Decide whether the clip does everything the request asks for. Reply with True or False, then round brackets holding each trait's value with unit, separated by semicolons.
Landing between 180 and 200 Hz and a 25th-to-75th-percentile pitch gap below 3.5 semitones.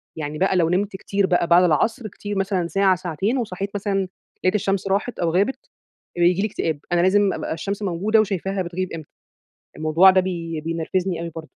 True (185 Hz; 2.7 semitones)